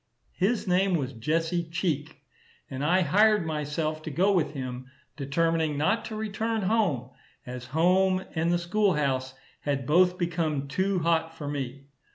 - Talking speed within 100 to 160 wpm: Yes, average, 155 wpm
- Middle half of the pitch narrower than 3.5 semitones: No, average, 4.6 semitones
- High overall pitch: No, medium, 165 Hz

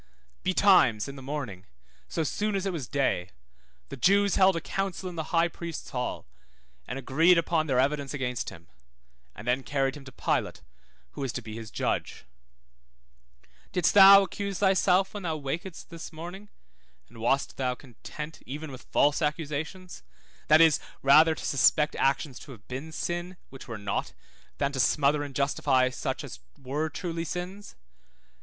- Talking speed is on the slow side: No, average, 165 wpm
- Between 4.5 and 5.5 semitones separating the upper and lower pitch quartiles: Yes, average, 4.8 semitones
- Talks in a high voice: No, medium, 150 Hz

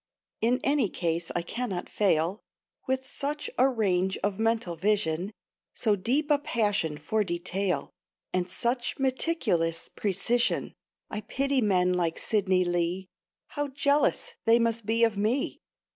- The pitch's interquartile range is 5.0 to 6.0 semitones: Yes, wide, 5.5 semitones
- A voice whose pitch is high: Yes, high, 210 Hz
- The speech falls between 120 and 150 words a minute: Yes, slow, 135 wpm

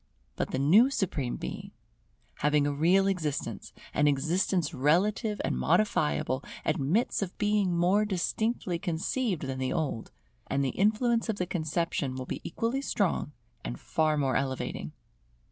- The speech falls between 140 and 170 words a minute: Yes, average, 145 wpm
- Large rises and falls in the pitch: Yes, wide, 6.1 semitones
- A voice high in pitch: No, medium, 170 Hz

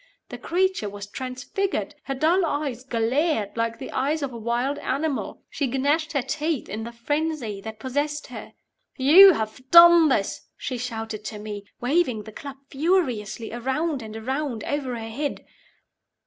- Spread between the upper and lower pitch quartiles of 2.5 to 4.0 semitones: No, average, 5.2 semitones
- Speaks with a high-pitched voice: Yes, very high, 260 Hz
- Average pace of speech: Yes, average, 160 wpm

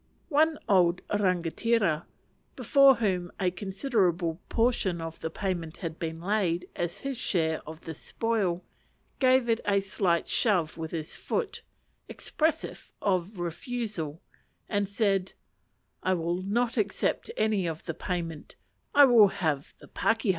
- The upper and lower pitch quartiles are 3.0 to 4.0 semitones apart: No, average, 4.9 semitones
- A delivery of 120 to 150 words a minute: Yes, slow, 135 wpm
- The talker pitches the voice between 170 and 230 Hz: Yes, high, 190 Hz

